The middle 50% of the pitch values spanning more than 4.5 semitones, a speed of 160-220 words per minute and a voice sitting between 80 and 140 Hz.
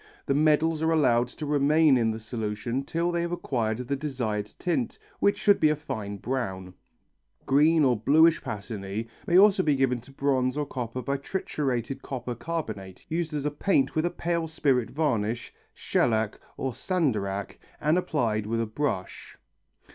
Yes: wide, 5.6 semitones; average, 165 wpm; low, 135 Hz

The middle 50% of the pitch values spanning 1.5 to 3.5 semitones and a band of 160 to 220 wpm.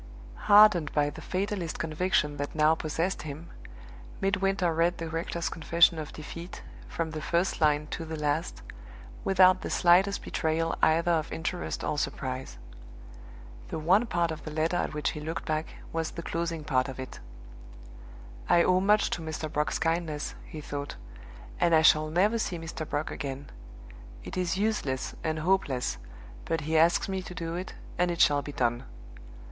Yes: narrow, 2.6 semitones; average, 170 wpm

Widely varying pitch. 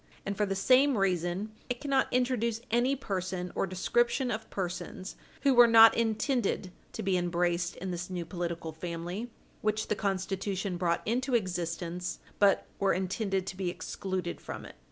No: average, 4.3 semitones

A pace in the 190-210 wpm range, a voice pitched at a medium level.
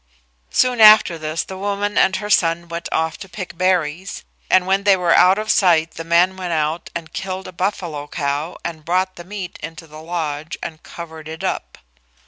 Yes: average, 195 wpm; medium, 175 Hz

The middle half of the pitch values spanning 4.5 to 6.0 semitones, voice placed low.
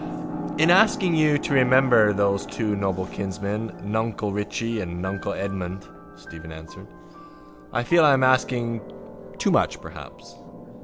Yes: average, 4.8 semitones; low, 105 Hz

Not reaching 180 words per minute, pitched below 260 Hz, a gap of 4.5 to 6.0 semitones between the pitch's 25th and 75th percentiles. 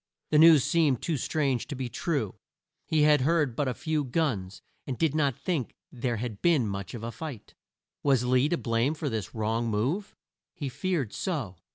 No: average, 190 wpm; low, 135 Hz; average, 5.1 semitones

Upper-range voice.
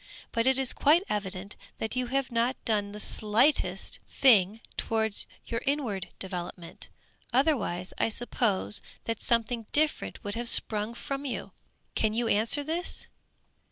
Yes: high, 230 Hz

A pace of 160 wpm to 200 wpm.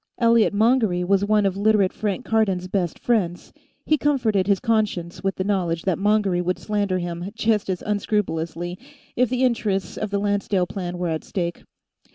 Yes: average, 175 wpm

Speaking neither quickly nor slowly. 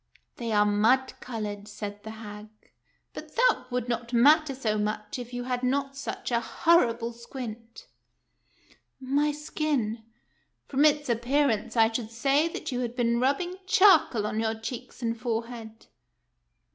Yes: average, 170 wpm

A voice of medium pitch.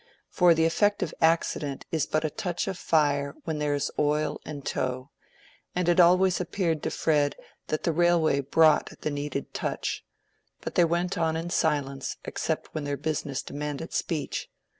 Yes: medium, 155 Hz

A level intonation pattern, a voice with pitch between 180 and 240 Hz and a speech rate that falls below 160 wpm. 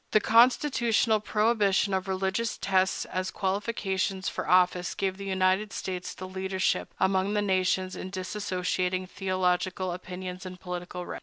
Yes: narrow, 1.4 semitones; high, 190 Hz; average, 140 wpm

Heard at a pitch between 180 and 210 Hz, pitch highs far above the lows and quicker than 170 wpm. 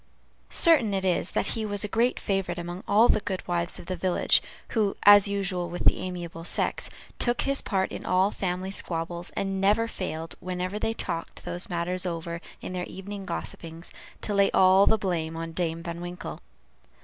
No: medium, 185 Hz; narrow, 2.6 semitones; average, 185 wpm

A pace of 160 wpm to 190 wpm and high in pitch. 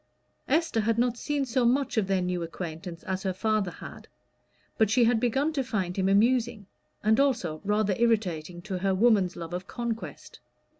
Yes: average, 180 wpm; high, 215 Hz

